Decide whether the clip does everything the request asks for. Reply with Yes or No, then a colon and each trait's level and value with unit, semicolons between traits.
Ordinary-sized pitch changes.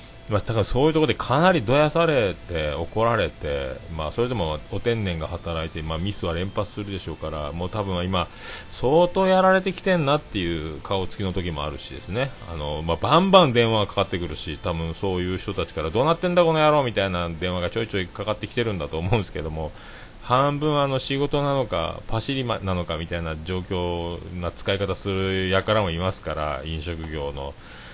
No: wide, 7.0 semitones